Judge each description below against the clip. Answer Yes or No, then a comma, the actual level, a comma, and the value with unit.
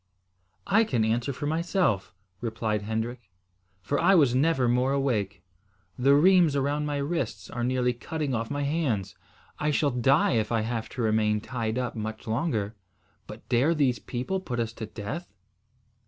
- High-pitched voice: No, low, 125 Hz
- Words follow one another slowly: No, average, 165 wpm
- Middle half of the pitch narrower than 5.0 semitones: Yes, average, 4.6 semitones